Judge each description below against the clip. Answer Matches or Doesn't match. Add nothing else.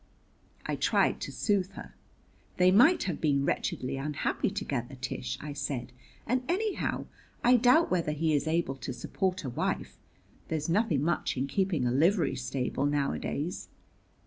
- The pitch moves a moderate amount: Doesn't match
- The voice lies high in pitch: Doesn't match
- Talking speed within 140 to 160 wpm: Matches